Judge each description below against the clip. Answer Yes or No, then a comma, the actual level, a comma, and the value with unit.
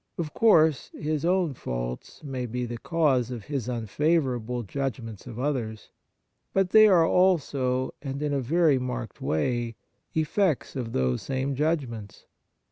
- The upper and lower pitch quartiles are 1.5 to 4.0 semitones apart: No, average, 4.7 semitones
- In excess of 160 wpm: No, average, 140 wpm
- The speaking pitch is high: No, low, 130 Hz